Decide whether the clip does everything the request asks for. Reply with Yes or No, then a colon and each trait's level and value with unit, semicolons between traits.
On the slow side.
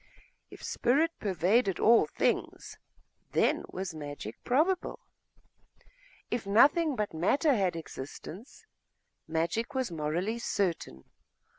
Yes: slow, 100 wpm